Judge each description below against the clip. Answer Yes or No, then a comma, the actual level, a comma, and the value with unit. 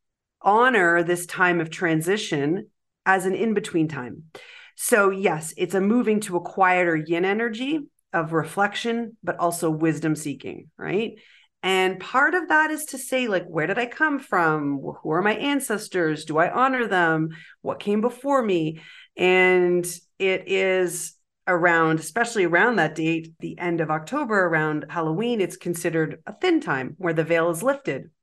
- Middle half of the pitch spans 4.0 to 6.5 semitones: Yes, average, 4.7 semitones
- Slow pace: No, average, 160 wpm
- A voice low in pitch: No, medium, 180 Hz